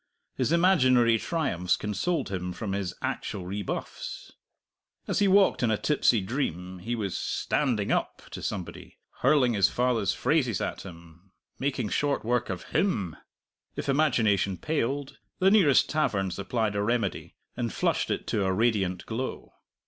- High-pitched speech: No, low, 115 Hz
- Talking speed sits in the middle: Yes, average, 150 wpm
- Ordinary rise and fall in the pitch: No, wide, 6.1 semitones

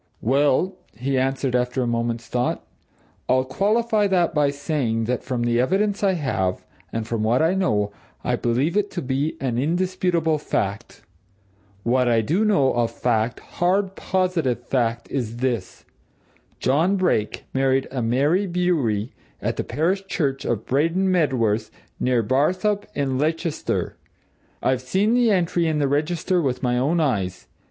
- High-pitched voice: No, low, 135 Hz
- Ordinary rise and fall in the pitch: No, wide, 6.6 semitones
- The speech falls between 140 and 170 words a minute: Yes, average, 150 wpm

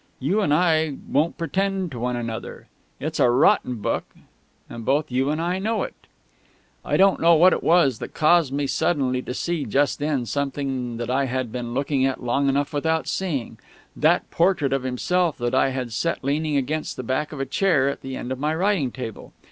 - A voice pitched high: No, medium, 140 Hz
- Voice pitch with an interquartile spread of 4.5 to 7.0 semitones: No, average, 4.0 semitones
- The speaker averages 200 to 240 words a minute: Yes, fast, 205 wpm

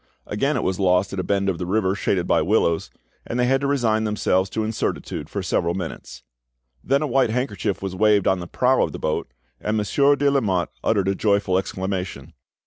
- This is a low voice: Yes, low, 100 Hz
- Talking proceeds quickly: Yes, fast, 210 wpm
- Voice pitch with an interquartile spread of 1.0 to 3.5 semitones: No, average, 4.2 semitones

